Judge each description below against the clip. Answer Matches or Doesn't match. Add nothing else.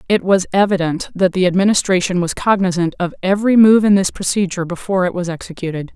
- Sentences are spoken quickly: Doesn't match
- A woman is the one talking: Matches